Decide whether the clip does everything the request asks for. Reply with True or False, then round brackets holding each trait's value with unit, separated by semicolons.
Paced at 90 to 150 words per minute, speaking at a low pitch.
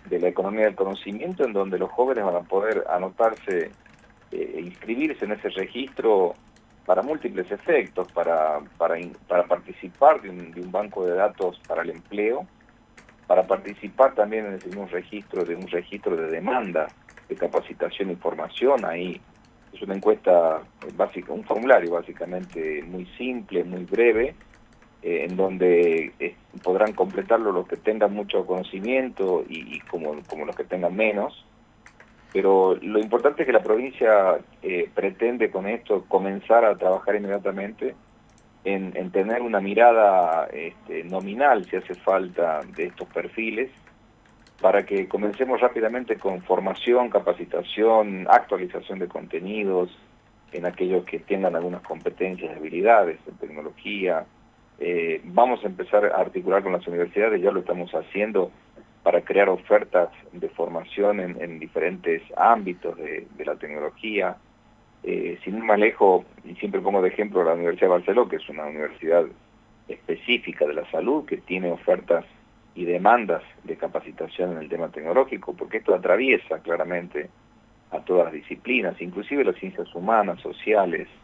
True (145 wpm; 110 Hz)